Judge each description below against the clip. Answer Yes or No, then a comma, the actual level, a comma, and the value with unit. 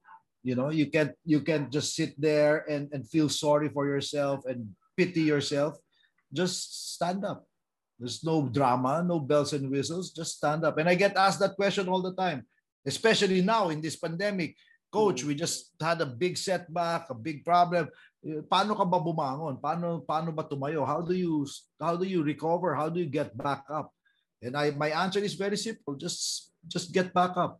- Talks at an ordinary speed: No, fast, 185 wpm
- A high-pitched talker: No, medium, 160 Hz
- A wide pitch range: No, average, 3.6 semitones